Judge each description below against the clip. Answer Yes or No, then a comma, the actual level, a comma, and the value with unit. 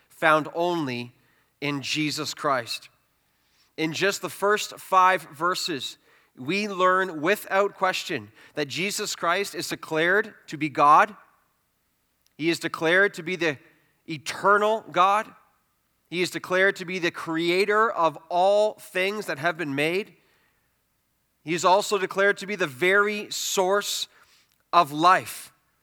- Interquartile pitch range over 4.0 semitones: No, average, 3.7 semitones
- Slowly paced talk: Yes, slow, 130 wpm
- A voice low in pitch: No, medium, 180 Hz